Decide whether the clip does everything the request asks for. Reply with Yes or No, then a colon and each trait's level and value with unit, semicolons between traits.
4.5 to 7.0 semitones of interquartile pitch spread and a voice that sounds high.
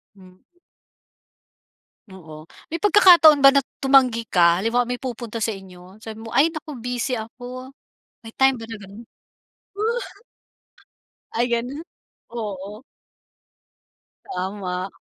Yes: average, 5.0 semitones; high, 230 Hz